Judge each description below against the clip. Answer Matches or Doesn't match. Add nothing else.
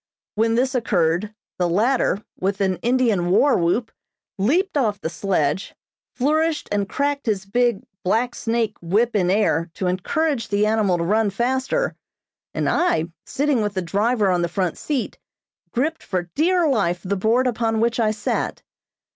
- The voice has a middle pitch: Doesn't match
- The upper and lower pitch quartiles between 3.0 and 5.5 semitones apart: Matches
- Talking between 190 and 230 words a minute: Doesn't match